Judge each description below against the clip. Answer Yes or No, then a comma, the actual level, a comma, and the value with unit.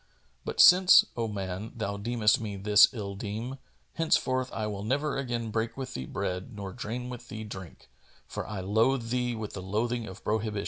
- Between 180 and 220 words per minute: Yes, average, 185 wpm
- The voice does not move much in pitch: No, average, 3.3 semitones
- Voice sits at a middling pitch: No, low, 110 Hz